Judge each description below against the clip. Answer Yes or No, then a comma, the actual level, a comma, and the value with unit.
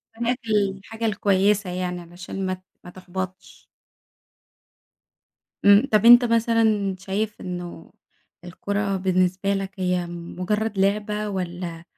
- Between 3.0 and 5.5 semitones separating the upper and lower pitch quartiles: No, narrow, 2.5 semitones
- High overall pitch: Yes, high, 195 Hz